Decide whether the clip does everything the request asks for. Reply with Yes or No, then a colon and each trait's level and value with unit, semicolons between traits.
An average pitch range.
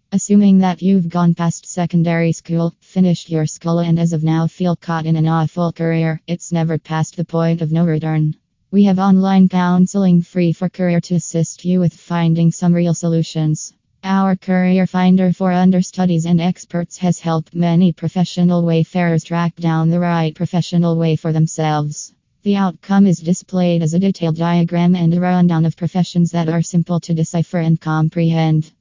No: narrow, 1.7 semitones